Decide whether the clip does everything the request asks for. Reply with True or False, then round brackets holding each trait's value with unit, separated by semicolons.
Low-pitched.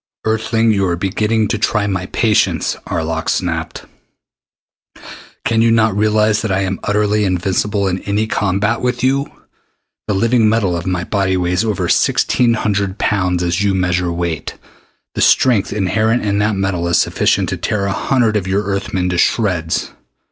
True (100 Hz)